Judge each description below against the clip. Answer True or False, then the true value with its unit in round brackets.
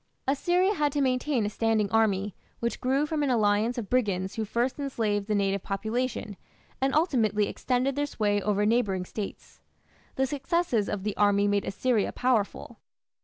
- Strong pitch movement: False (4.5 semitones)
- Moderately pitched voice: False (225 Hz)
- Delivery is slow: False (165 wpm)